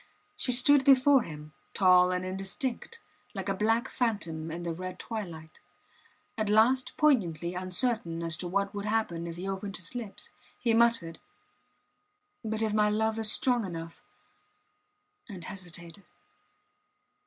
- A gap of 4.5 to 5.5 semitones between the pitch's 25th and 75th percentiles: Yes, average, 4.8 semitones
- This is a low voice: No, high, 200 Hz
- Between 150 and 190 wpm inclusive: No, average, 140 wpm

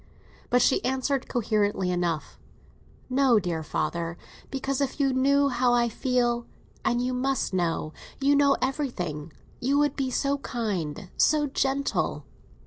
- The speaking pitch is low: No, very high, 250 Hz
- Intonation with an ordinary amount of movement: No, wide, 5.9 semitones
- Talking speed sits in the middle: No, slow, 125 wpm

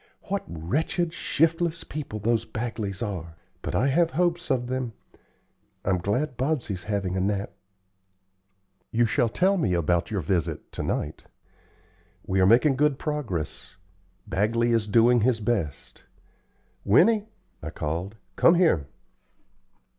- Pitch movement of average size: No, wide, 7.8 semitones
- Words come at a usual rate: No, slow, 130 wpm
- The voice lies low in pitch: Yes, low, 115 Hz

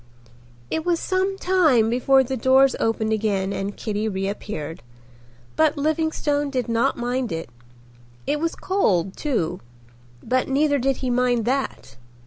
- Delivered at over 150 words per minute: No, slow, 135 wpm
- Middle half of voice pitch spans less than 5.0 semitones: No, average, 5.3 semitones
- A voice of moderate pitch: No, very high, 255 Hz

